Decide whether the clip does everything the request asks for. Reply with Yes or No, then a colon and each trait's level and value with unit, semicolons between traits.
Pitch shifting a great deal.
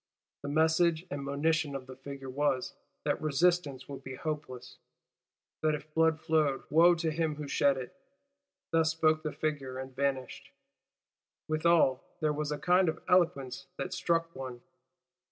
No: average, 2.9 semitones